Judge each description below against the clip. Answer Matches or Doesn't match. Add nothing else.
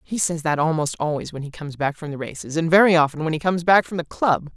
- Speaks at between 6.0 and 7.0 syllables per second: Matches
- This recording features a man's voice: Doesn't match